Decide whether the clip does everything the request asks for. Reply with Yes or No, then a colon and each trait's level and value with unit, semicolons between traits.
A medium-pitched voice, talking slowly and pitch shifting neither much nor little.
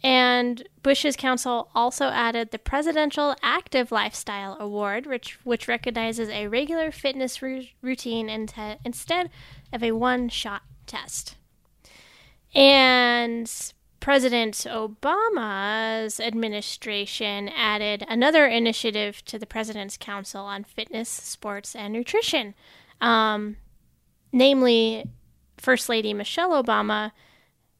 No: high, 230 Hz; slow, 105 wpm; average, 3.4 semitones